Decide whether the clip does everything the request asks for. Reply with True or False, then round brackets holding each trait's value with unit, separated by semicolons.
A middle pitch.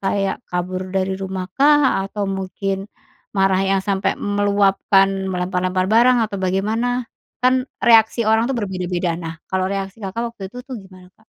False (195 Hz)